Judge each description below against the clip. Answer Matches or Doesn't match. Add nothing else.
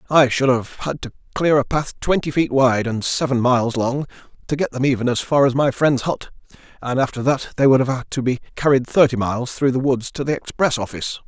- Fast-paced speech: Matches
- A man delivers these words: Matches